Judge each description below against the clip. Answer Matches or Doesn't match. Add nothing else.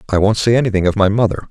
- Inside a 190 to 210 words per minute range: Doesn't match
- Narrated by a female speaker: Doesn't match